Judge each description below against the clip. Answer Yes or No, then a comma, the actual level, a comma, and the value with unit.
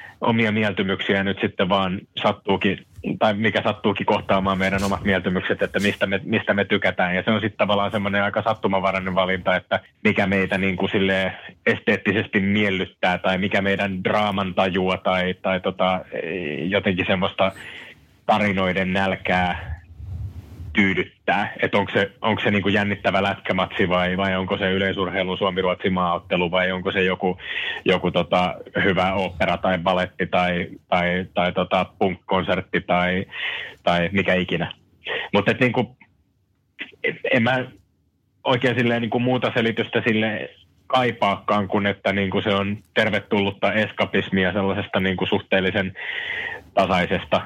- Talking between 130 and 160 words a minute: Yes, average, 135 wpm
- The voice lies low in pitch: Yes, very low, 95 Hz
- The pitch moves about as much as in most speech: No, narrow, 1.8 semitones